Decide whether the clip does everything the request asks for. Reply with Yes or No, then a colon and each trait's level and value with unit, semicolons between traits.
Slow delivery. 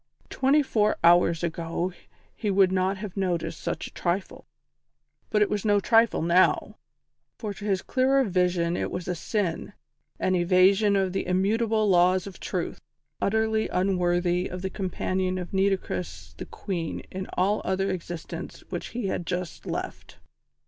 No: average, 155 wpm